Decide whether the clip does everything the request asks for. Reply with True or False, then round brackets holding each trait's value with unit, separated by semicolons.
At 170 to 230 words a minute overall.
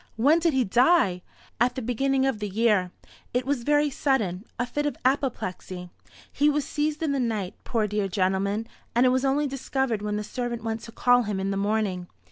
True (205 wpm)